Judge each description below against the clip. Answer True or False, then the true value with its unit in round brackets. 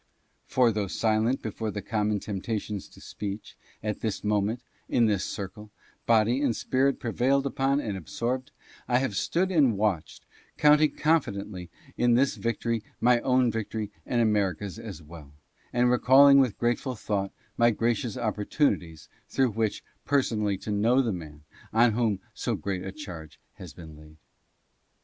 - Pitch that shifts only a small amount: False (3.8 semitones)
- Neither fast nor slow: True (155 wpm)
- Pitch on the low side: True (110 Hz)